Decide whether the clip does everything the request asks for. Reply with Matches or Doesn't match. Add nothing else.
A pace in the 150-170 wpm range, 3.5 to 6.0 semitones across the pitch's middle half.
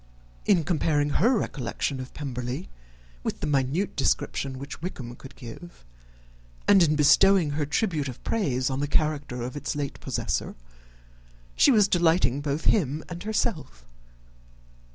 Doesn't match